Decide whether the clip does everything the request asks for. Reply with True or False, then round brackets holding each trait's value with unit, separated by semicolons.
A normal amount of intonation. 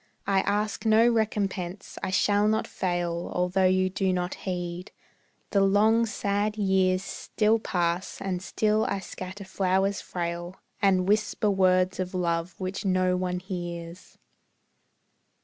False (2.0 semitones)